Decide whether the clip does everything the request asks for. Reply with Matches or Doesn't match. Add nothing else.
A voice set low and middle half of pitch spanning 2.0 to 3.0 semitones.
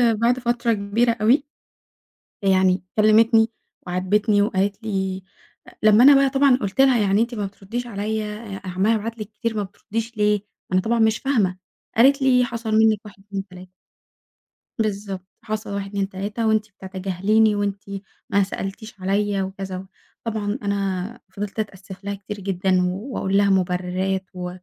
Doesn't match